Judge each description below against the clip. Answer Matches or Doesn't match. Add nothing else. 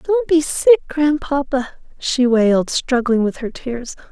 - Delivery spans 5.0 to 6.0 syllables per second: Doesn't match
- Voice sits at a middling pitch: Doesn't match